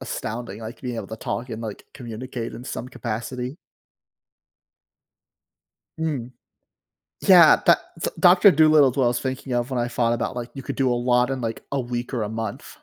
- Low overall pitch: Yes, low, 125 Hz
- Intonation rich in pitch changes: No, narrow, 2.5 semitones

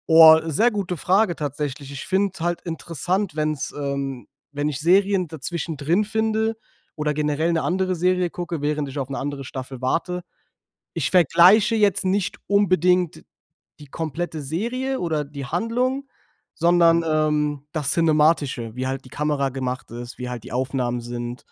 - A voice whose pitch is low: No, medium, 160 Hz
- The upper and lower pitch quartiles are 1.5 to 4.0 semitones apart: No, average, 4.7 semitones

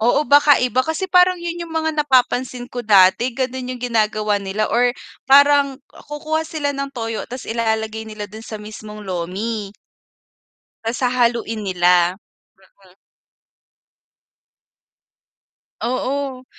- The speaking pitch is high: Yes, high, 245 Hz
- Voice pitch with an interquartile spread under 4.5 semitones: No, average, 4.8 semitones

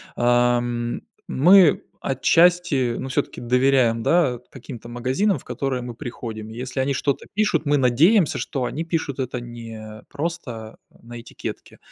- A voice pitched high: No, low, 130 Hz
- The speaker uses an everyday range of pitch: Yes, average, 3.7 semitones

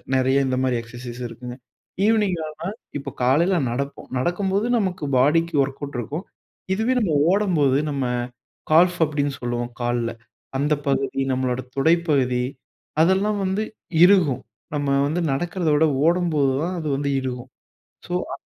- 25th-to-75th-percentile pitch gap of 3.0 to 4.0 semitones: No, wide, 5.4 semitones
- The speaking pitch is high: No, medium, 145 Hz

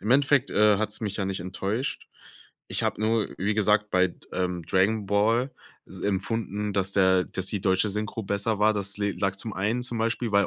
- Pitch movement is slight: Yes, narrow, 2.3 semitones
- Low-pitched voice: Yes, low, 105 Hz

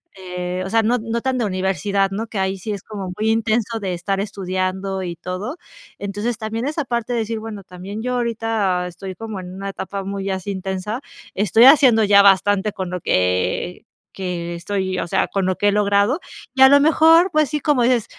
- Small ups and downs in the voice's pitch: No, average, 3.3 semitones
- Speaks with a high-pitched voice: Yes, high, 200 Hz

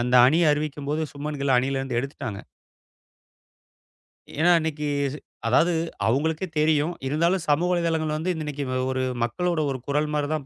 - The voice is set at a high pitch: No, medium, 150 Hz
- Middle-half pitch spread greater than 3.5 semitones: No, average, 2.7 semitones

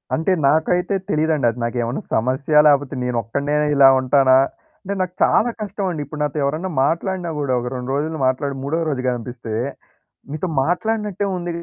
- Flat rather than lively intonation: No, average, 5.1 semitones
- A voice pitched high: No, medium, 150 Hz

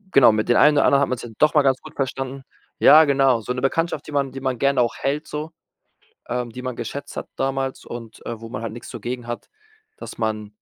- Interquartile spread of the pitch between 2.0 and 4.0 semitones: Yes, average, 2.7 semitones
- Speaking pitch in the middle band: No, low, 130 Hz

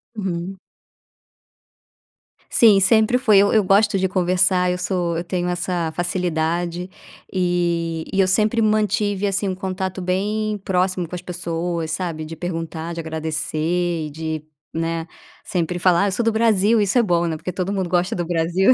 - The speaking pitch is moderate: Yes, medium, 180 Hz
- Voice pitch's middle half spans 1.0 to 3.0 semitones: Yes, narrow, 2.5 semitones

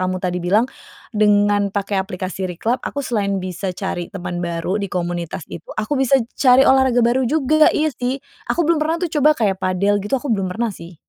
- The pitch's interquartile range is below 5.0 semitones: No, wide, 5.6 semitones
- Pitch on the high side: Yes, high, 205 Hz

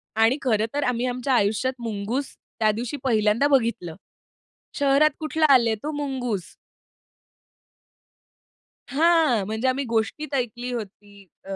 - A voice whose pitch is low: No, high, 245 Hz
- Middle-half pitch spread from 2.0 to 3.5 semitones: No, average, 4.1 semitones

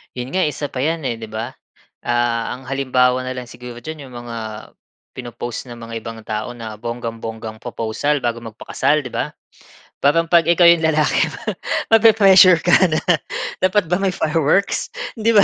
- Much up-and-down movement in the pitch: Yes, wide, 5.8 semitones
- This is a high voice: No, low, 130 Hz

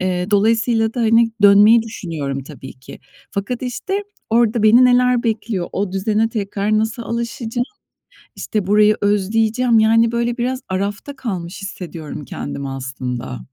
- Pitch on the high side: Yes, high, 215 Hz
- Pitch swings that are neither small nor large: Yes, average, 3.7 semitones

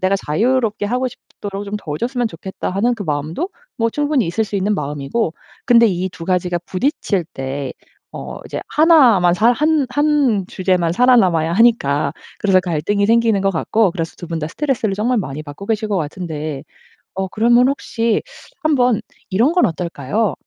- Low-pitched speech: No, high, 200 Hz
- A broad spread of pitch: Yes, wide, 5.9 semitones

